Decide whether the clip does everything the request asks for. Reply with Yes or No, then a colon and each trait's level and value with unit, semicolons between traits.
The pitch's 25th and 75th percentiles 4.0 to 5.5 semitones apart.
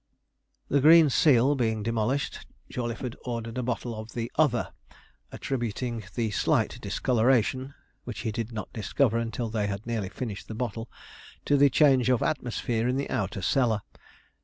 No: narrow, 2.6 semitones